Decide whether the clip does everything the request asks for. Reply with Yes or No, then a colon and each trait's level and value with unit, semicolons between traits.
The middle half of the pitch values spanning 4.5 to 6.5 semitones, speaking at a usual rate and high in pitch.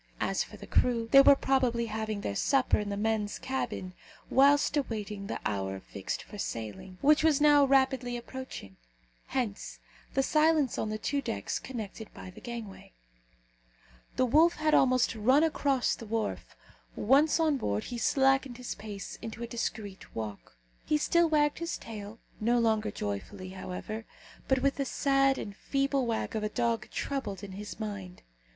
Yes: average, 4.8 semitones; average, 165 wpm; high, 235 Hz